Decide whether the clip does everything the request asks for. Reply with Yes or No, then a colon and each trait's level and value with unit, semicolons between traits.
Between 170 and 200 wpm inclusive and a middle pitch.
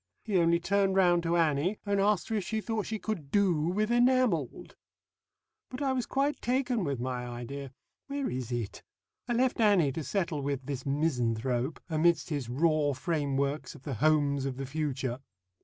Yes: average, 175 wpm; medium, 160 Hz